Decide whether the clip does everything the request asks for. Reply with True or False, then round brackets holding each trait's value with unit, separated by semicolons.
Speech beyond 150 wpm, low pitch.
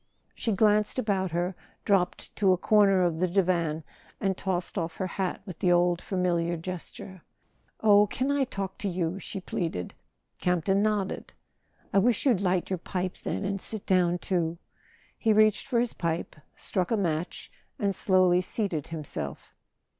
False (165 wpm; 185 Hz)